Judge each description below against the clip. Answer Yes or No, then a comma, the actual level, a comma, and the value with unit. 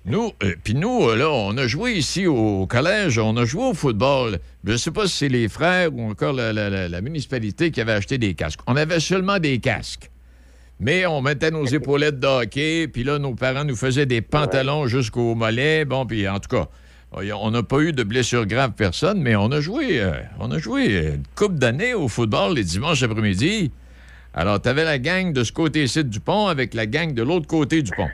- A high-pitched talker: No, low, 130 Hz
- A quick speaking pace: Yes, fast, 225 wpm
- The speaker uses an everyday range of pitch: No, wide, 6.0 semitones